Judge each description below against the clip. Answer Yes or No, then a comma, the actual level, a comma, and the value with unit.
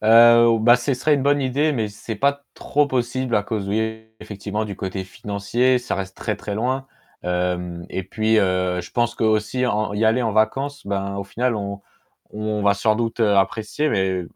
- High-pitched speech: No, low, 110 Hz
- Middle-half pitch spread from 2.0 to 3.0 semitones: No, average, 3.5 semitones